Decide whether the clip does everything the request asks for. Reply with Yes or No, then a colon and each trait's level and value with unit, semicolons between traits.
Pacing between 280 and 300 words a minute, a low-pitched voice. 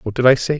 No: fast, 405 wpm; low, 130 Hz